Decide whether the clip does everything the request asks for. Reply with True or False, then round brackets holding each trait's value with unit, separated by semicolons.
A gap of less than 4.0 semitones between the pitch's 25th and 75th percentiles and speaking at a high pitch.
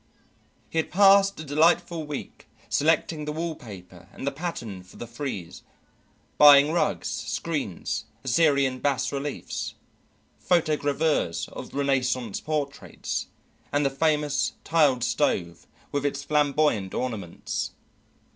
False (3.6 semitones; 145 Hz)